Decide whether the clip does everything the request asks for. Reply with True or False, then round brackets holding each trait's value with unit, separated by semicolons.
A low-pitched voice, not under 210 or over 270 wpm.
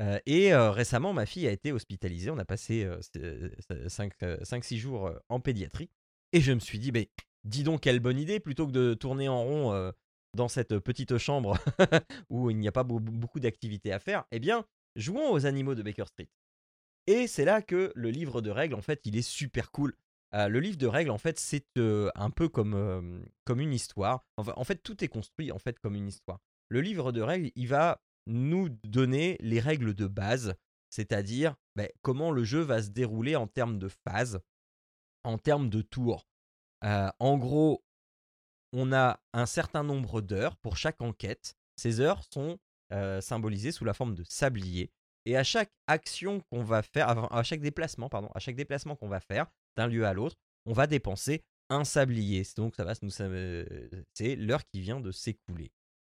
False (120 Hz; 190 wpm)